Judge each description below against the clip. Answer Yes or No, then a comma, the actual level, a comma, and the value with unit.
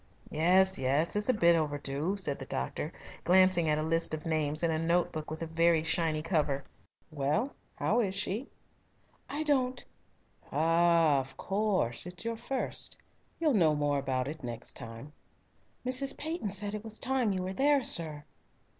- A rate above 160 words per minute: Yes, average, 170 wpm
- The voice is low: No, medium, 170 Hz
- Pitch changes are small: No, wide, 5.4 semitones